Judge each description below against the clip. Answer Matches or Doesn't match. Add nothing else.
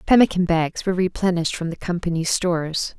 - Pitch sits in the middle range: Matches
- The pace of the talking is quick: Doesn't match